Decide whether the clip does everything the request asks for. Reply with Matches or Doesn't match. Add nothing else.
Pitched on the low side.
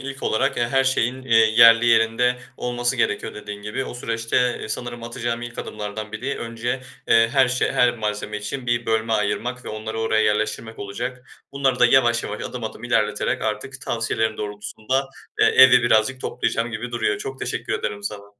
Matches